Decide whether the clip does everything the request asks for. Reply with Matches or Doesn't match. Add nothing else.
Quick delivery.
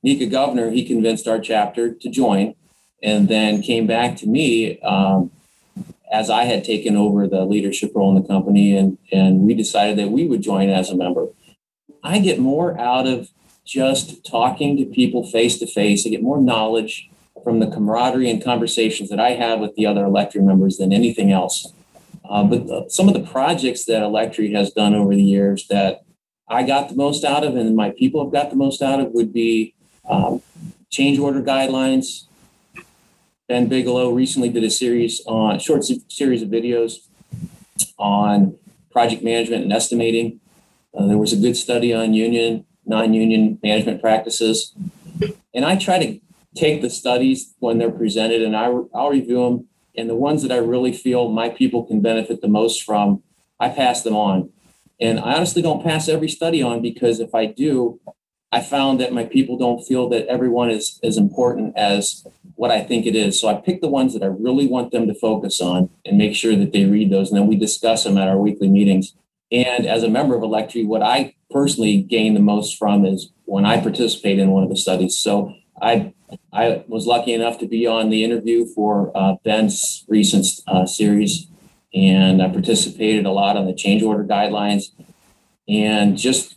Doesn't match